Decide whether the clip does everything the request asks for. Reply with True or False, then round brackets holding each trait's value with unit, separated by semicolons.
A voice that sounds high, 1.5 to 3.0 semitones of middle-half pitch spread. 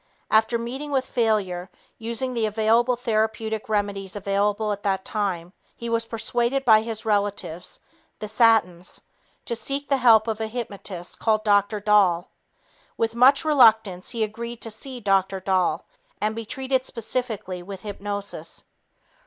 True (220 Hz; 2.6 semitones)